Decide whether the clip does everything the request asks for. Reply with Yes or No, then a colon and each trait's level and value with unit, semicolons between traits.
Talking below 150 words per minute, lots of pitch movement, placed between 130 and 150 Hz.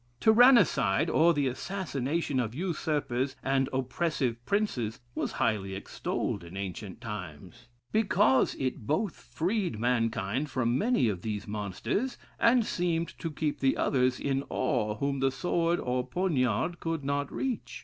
Yes: average, 140 wpm; wide, 6.5 semitones; low, 135 Hz